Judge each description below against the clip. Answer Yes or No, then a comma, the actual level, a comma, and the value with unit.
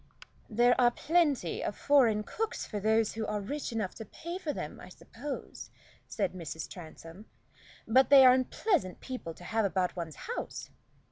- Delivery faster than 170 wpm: No, average, 165 wpm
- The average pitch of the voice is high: Yes, high, 225 Hz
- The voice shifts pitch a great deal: Yes, wide, 6.7 semitones